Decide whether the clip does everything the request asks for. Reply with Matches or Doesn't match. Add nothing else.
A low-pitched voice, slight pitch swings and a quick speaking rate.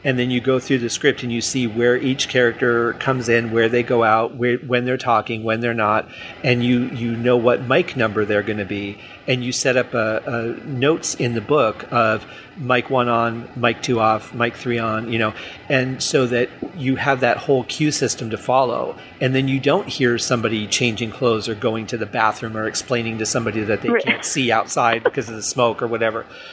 Matches